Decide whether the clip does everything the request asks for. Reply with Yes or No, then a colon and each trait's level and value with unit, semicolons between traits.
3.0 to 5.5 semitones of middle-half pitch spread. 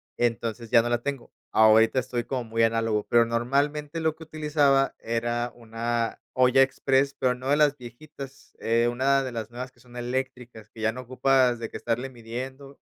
No: narrow, 2.6 semitones